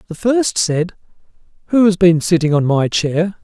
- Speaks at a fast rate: No, average, 175 wpm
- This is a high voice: No, medium, 175 Hz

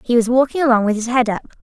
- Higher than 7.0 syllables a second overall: Yes, 7.2 syllables/s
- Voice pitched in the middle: No, high, 240 Hz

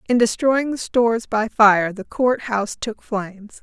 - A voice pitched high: Yes, high, 225 Hz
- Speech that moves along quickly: No, average, 180 wpm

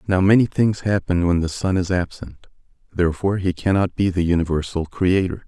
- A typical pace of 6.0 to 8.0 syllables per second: No, 5.6 syllables/s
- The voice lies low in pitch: Yes, very low, 90 Hz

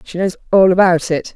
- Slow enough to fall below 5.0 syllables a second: No, 5.4 syllables/s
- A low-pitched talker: No, medium, 180 Hz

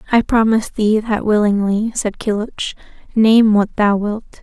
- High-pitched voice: Yes, high, 215 Hz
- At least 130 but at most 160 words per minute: Yes, average, 150 wpm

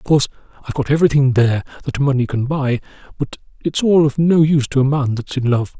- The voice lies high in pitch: No, medium, 140 Hz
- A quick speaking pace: Yes, fast, 215 wpm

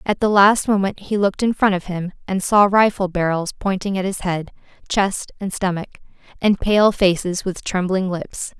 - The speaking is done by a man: No, female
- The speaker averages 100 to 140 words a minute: No, average, 190 wpm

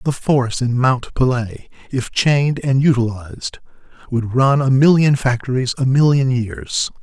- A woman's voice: No, male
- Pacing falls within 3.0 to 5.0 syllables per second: Yes, 4.4 syllables/s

